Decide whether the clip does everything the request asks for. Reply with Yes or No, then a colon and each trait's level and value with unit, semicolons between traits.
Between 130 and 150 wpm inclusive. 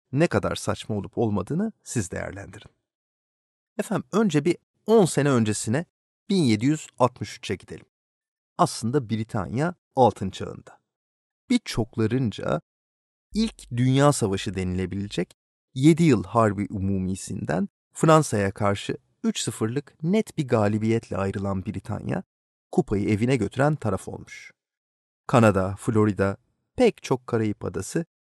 No: average, 100 wpm